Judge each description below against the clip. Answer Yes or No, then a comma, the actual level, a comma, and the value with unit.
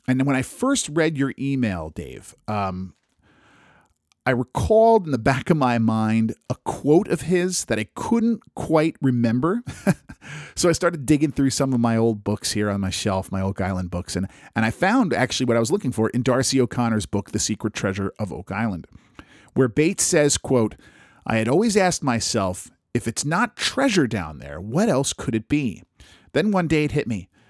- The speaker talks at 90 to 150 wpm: No, average, 195 wpm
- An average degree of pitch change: No, wide, 6.3 semitones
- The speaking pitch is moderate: No, low, 125 Hz